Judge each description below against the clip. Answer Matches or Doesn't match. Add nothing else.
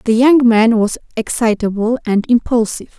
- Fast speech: Doesn't match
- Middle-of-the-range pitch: Doesn't match